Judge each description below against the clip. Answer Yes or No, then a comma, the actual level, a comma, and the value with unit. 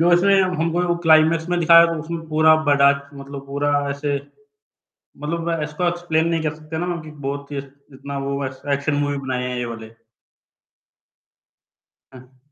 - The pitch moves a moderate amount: Yes, average, 3.1 semitones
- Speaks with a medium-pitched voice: Yes, medium, 155 Hz